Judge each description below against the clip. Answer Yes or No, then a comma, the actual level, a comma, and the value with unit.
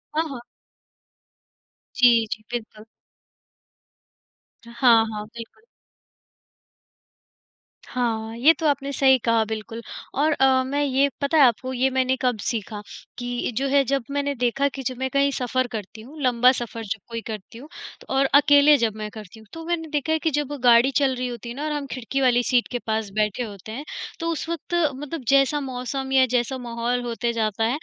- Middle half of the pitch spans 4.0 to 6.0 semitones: No, average, 3.3 semitones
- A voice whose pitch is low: No, very high, 255 Hz